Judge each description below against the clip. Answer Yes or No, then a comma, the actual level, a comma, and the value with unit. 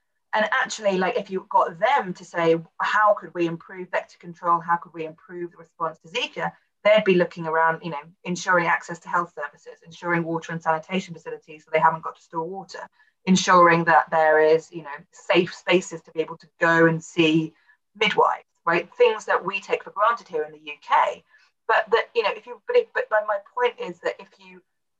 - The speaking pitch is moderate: Yes, medium, 170 Hz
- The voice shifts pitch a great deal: No, average, 3.0 semitones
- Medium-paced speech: No, fast, 210 wpm